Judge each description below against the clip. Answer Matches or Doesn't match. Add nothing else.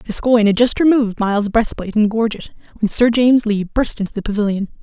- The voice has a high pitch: Matches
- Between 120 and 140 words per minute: Doesn't match